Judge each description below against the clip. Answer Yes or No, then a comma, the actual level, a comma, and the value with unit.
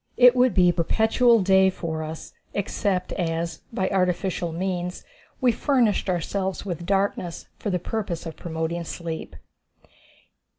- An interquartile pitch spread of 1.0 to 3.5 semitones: Yes, average, 3.0 semitones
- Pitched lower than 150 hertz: No, medium, 180 Hz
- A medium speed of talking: No, slow, 130 wpm